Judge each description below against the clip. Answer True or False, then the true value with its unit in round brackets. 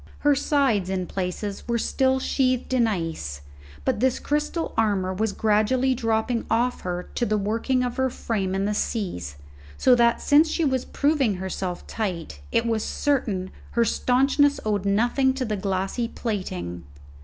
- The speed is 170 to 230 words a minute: False (160 wpm)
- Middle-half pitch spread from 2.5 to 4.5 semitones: False (5.2 semitones)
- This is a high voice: True (225 Hz)